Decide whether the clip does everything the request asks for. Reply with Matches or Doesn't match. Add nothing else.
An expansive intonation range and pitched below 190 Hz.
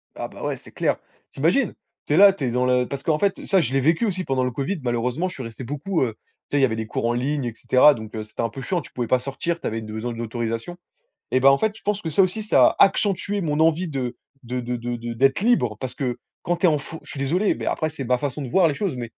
Matches